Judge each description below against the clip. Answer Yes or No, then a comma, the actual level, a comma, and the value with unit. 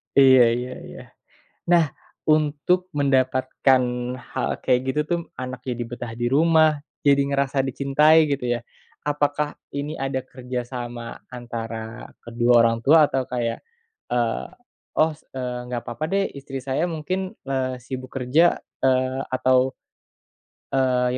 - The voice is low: Yes, low, 130 Hz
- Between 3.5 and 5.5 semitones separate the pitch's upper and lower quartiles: No, average, 3.0 semitones